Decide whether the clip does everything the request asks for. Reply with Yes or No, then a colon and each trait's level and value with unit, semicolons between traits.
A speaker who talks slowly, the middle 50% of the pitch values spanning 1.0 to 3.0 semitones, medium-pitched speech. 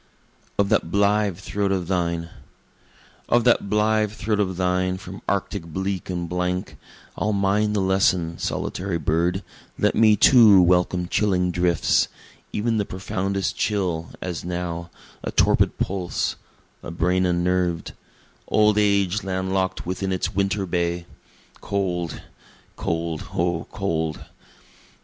No: slow, 125 wpm; narrow, 2.4 semitones; very low, 95 Hz